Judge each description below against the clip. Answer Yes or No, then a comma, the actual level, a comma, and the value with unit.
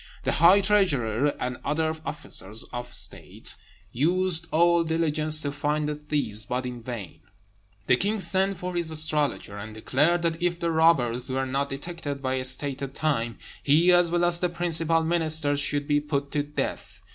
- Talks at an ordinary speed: Yes, average, 170 wpm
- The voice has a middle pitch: Yes, medium, 150 Hz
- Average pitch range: Yes, average, 4.2 semitones